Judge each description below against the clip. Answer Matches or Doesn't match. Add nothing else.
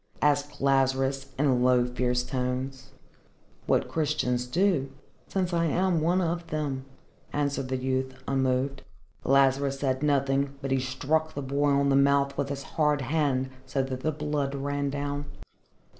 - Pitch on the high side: Doesn't match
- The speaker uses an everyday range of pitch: Doesn't match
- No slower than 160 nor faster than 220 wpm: Doesn't match